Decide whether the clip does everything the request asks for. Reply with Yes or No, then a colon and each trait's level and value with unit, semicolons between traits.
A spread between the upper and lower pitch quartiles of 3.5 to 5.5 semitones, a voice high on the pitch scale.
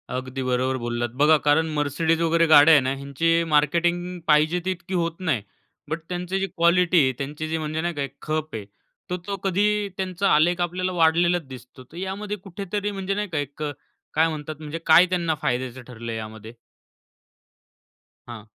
No: average, 3.9 semitones; medium, 160 Hz